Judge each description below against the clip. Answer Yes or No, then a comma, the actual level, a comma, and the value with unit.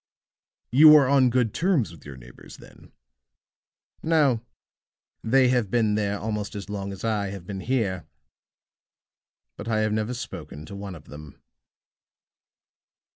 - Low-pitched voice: Yes, low, 110 Hz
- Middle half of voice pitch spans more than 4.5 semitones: No, average, 4.2 semitones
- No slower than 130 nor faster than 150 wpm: Yes, average, 140 wpm